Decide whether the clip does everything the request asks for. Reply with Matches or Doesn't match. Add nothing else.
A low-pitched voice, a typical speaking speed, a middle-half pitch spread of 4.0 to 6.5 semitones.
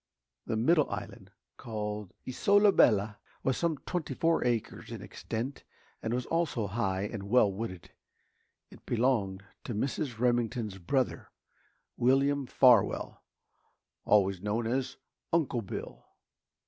Doesn't match